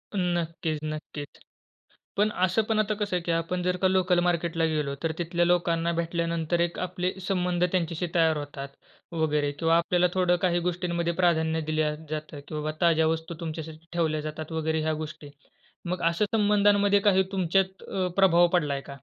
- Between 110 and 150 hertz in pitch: No, medium, 170 Hz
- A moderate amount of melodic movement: No, narrow, 2.3 semitones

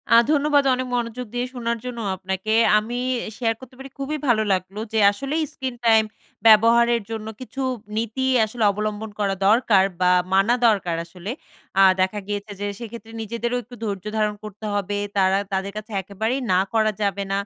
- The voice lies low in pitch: No, high, 220 Hz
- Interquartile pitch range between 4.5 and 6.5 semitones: No, average, 3.1 semitones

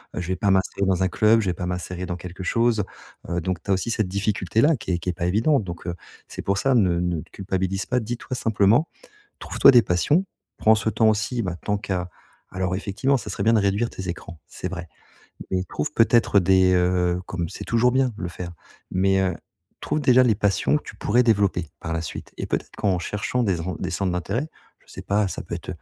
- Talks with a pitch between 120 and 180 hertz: No, very low, 95 Hz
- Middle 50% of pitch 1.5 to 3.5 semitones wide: No, average, 3.9 semitones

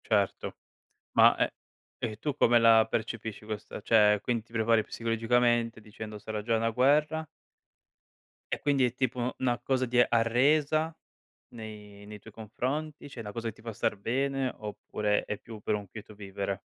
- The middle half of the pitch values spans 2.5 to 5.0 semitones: Yes, average, 2.8 semitones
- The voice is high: No, low, 115 Hz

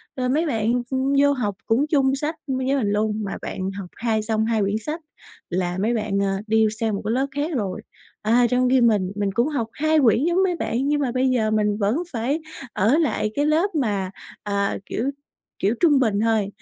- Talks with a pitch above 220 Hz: Yes, high, 235 Hz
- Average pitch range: Yes, average, 4.7 semitones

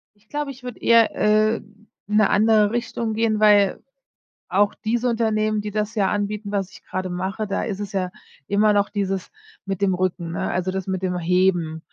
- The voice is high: Yes, high, 205 Hz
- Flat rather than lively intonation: Yes, narrow, 2.3 semitones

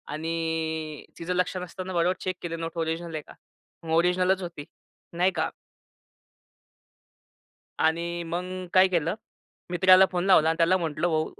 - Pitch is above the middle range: No, medium, 170 Hz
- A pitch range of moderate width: No, narrow, 2.0 semitones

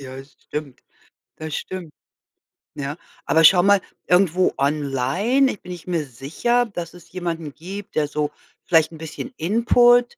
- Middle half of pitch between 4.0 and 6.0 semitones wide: Yes, average, 4.8 semitones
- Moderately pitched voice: Yes, medium, 165 Hz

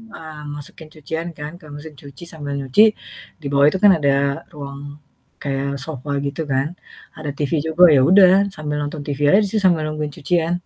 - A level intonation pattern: Yes, narrow, 2.3 semitones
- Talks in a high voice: No, medium, 150 Hz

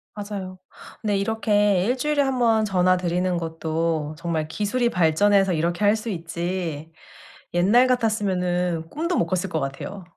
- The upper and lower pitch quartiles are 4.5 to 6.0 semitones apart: No, average, 4.0 semitones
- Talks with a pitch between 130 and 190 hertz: Yes, medium, 185 Hz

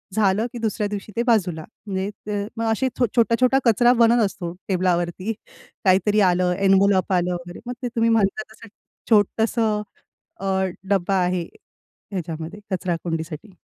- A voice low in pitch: No, high, 195 Hz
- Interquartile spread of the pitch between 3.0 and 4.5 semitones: Yes, average, 3.8 semitones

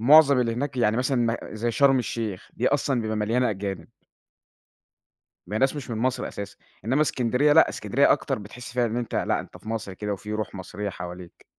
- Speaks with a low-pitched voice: Yes, low, 115 Hz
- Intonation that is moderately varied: Yes, average, 3.6 semitones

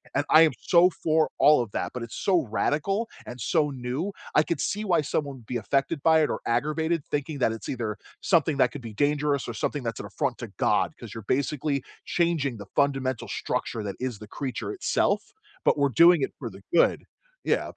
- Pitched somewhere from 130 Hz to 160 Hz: Yes, medium, 140 Hz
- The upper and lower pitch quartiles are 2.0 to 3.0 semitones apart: No, average, 4.5 semitones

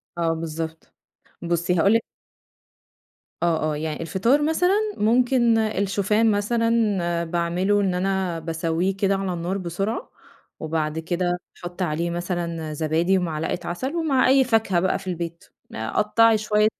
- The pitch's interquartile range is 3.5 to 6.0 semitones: Yes, average, 4.1 semitones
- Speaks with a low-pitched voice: No, medium, 180 Hz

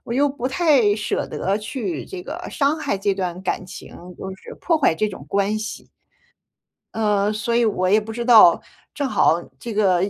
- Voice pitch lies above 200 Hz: Yes, high, 215 Hz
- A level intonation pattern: No, average, 4.8 semitones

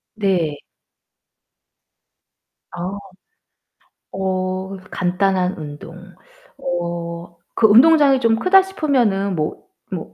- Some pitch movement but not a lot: Yes, average, 4.5 semitones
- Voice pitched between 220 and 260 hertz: No, high, 190 Hz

